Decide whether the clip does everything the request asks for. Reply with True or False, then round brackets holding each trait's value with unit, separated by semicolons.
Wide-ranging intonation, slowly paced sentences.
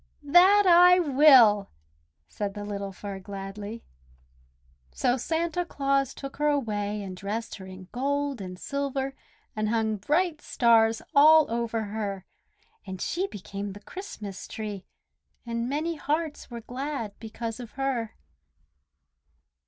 True (5.8 semitones; 130 wpm)